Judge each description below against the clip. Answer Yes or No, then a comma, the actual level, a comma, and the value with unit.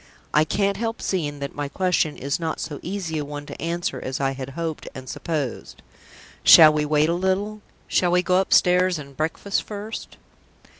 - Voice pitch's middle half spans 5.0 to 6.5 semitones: No, average, 4.1 semitones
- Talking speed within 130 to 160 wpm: No, average, 185 wpm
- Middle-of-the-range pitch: Yes, medium, 160 Hz